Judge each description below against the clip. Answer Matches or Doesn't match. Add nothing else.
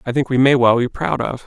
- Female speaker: Doesn't match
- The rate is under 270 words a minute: Doesn't match